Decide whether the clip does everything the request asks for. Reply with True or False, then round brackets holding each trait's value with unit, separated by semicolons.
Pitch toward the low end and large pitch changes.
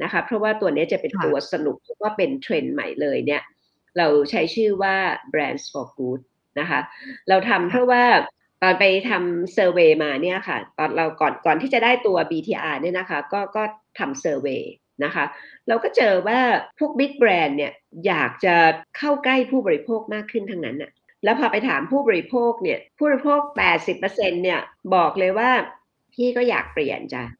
False (200 Hz; 6.2 semitones)